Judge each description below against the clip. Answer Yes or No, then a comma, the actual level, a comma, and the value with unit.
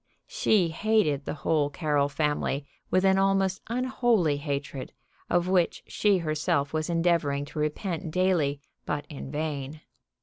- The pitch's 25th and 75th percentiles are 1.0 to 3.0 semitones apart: No, average, 4.6 semitones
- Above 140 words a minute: No, slow, 135 wpm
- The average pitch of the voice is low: No, medium, 160 Hz